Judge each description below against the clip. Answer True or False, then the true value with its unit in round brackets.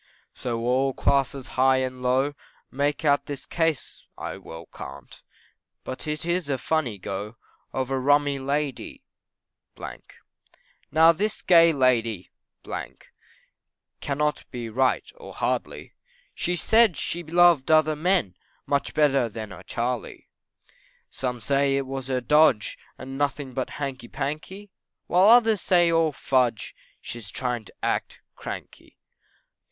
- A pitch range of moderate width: True (3.8 semitones)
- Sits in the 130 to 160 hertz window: True (135 Hz)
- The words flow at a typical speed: False (130 wpm)